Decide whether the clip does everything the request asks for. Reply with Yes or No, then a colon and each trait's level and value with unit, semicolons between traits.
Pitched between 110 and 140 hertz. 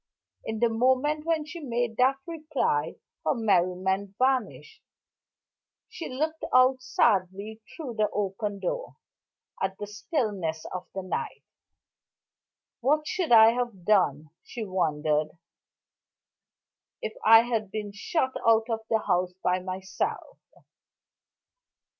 No: high, 220 Hz